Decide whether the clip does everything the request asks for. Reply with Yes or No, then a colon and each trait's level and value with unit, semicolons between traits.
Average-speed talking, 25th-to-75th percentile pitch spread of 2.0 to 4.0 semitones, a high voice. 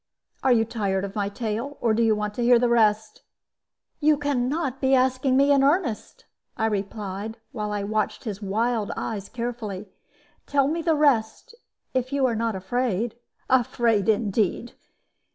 Yes: average, 165 wpm; average, 3.7 semitones; high, 230 Hz